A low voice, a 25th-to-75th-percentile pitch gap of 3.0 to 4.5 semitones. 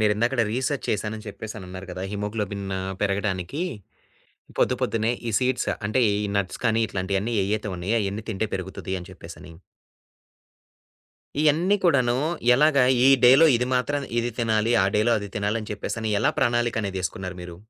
Yes: low, 110 Hz; average, 3.6 semitones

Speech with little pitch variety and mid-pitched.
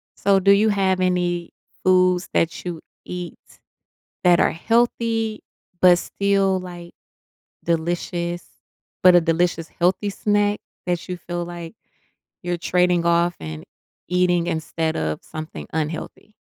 Yes: narrow, 1.7 semitones; medium, 175 Hz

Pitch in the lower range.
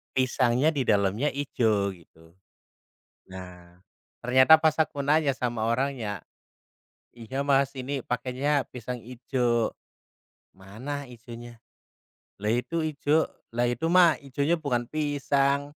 Yes: low, 130 Hz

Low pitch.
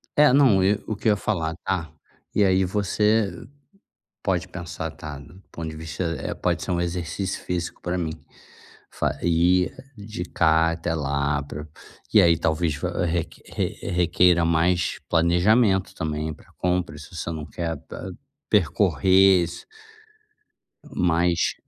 Yes: very low, 85 Hz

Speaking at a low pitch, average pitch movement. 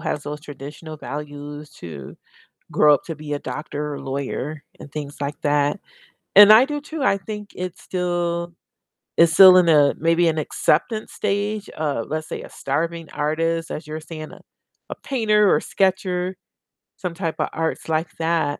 No: medium, 160 Hz; average, 3.7 semitones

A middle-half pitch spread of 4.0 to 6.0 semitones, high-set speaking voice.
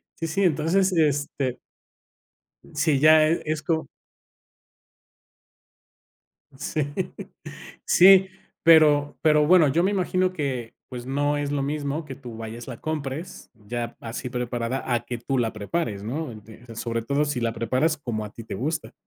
No: average, 4.7 semitones; medium, 140 Hz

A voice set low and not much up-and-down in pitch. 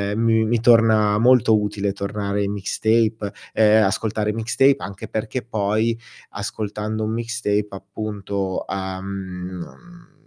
Yes: low, 105 Hz; narrow, 2.2 semitones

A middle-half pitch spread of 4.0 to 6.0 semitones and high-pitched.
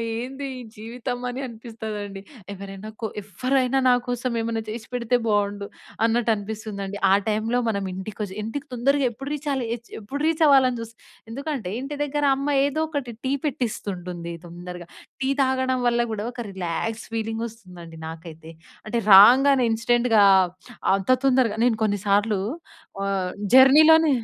Yes: average, 4.4 semitones; high, 225 Hz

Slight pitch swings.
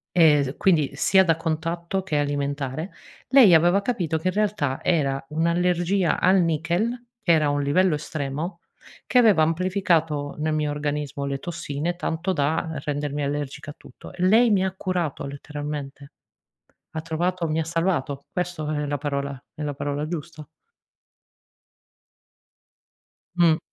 No: average, 3.5 semitones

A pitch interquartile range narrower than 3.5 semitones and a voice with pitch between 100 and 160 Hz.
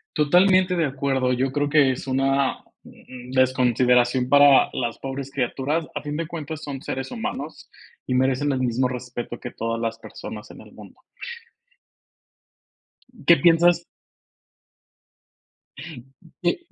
Yes: average, 2.9 semitones; low, 135 Hz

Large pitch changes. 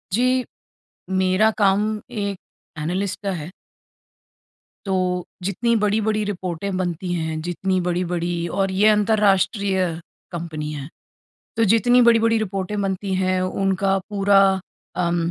No: narrow, 2.6 semitones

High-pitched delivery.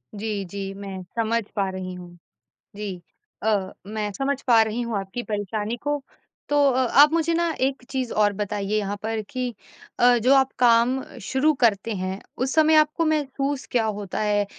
Yes: high, 225 Hz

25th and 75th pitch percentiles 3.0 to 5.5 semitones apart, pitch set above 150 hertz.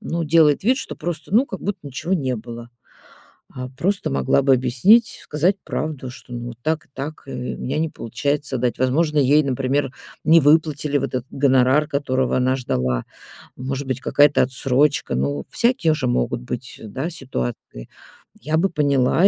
No: average, 3.6 semitones; medium, 140 Hz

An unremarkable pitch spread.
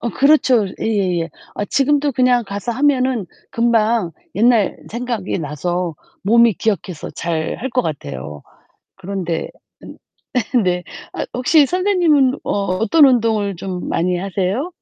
No: wide, 5.8 semitones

